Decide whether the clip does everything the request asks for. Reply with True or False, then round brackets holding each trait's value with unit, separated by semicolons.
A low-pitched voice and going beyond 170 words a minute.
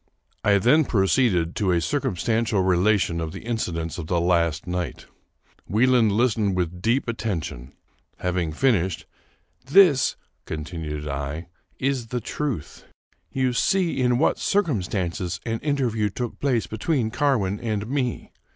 False (105 Hz; 140 wpm)